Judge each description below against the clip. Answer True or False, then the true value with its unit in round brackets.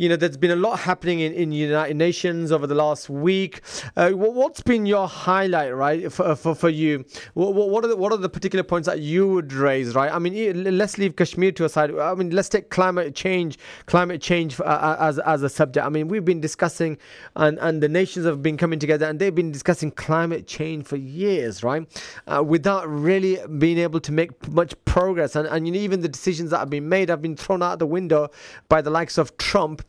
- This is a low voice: False (170 Hz)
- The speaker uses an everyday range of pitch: True (3.2 semitones)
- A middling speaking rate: False (225 wpm)